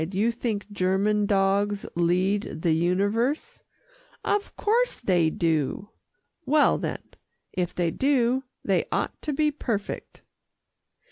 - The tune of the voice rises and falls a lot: Yes, wide, 5.7 semitones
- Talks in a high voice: Yes, high, 205 Hz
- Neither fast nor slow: No, slow, 115 wpm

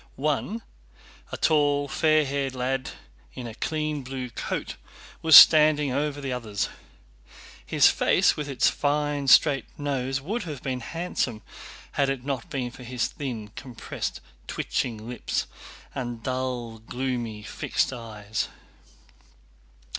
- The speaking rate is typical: No, slow, 125 wpm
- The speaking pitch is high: No, low, 135 Hz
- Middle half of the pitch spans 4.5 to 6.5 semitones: No, average, 3.0 semitones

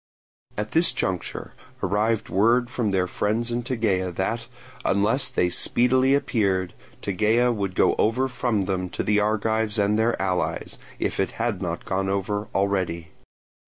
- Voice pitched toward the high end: No, low, 105 Hz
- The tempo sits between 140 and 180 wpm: Yes, average, 150 wpm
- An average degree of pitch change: Yes, average, 3.4 semitones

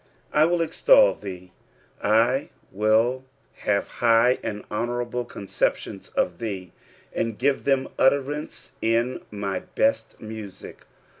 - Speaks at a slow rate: Yes, slow, 115 wpm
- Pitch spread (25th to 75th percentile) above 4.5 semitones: No, average, 4.2 semitones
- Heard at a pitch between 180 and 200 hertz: No, low, 115 Hz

